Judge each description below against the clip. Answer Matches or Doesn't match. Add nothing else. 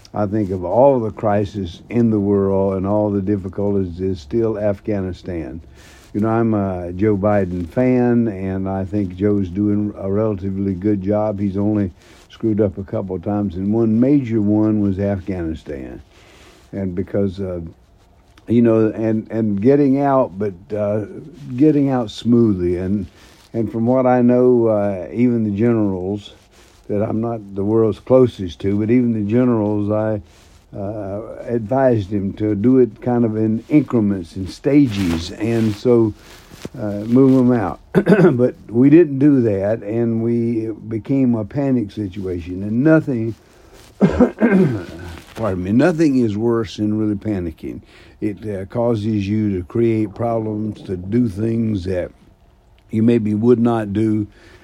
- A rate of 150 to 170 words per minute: Matches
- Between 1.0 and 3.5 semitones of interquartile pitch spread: Matches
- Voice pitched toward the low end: Matches